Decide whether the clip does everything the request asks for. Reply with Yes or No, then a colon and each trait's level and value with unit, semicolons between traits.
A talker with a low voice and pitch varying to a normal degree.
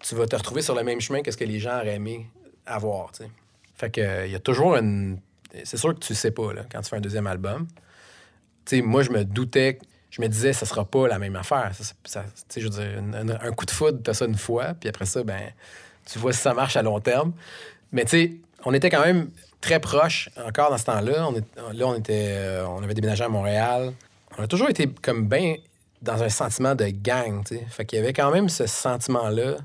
Yes: low, 115 Hz; average, 3.6 semitones